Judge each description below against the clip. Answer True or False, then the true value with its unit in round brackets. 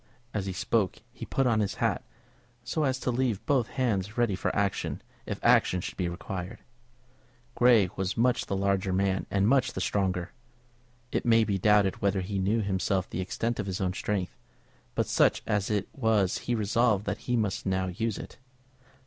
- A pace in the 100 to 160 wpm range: False (190 wpm)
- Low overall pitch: True (100 Hz)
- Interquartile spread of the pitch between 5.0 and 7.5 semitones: False (3.4 semitones)